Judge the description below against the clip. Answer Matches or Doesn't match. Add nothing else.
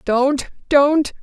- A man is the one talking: Doesn't match